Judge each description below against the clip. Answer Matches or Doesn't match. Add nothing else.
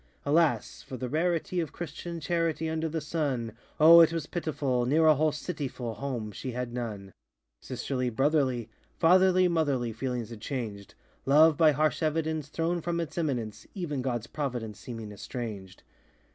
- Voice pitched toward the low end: Doesn't match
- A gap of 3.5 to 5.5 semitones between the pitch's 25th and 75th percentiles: Matches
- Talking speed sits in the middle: Matches